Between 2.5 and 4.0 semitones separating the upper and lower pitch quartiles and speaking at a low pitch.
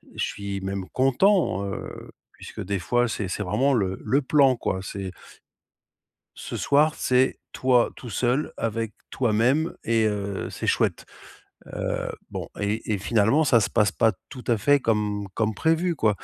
No: average, 4.4 semitones; low, 115 Hz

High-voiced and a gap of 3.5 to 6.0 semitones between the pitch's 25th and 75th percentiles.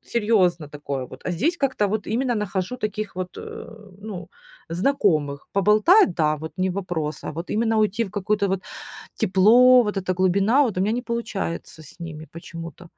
Yes: high, 195 Hz; average, 4.5 semitones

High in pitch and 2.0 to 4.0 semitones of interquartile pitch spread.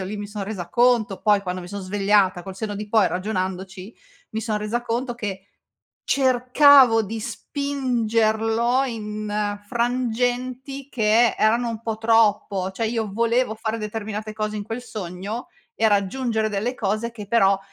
Yes: high, 220 Hz; narrow, 2.6 semitones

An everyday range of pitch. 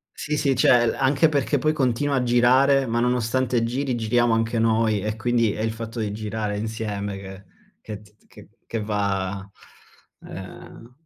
Yes: average, 3.0 semitones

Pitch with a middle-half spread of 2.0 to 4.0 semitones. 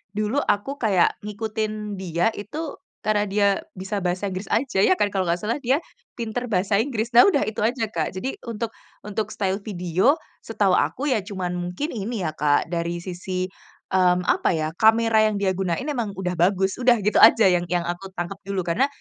Yes: average, 3.7 semitones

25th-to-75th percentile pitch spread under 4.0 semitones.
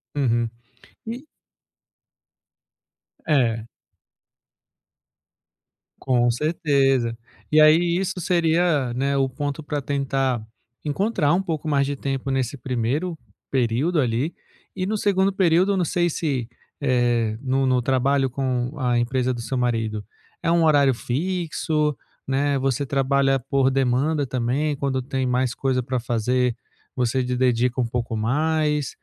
Yes: average, 3.6 semitones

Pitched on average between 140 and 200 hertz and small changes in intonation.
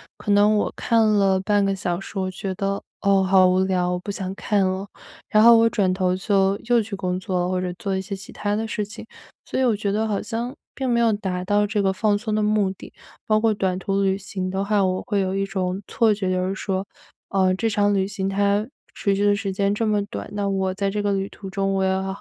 Yes: high, 195 Hz; narrow, 1.6 semitones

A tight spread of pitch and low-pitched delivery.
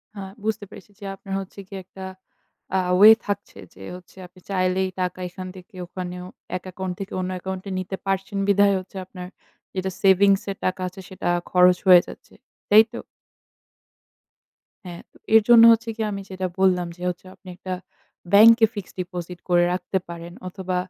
No: narrow, 1.6 semitones; high, 190 Hz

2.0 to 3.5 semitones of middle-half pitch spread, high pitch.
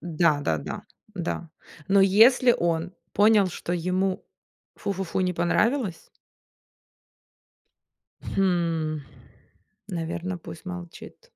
No: narrow, 2.6 semitones; medium, 180 Hz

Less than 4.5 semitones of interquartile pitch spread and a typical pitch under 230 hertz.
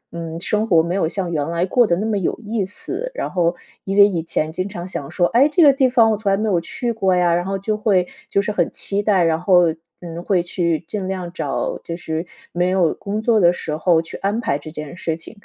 Yes: average, 3.8 semitones; medium, 185 Hz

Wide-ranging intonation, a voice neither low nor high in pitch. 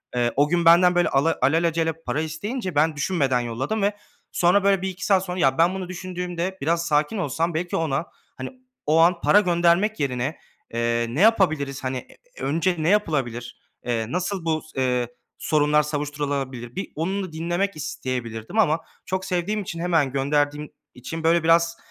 No: average, 4.4 semitones; medium, 165 Hz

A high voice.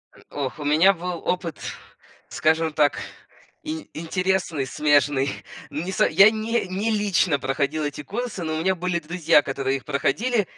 No: medium, 165 Hz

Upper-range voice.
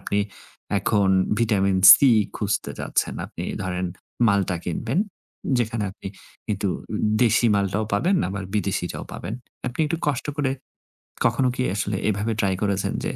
No: low, 105 Hz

